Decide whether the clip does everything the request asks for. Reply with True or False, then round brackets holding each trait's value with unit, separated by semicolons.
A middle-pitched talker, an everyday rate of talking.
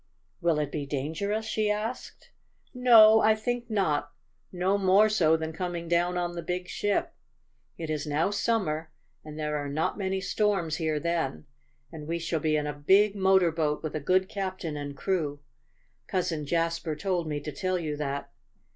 True (170 Hz; 175 wpm)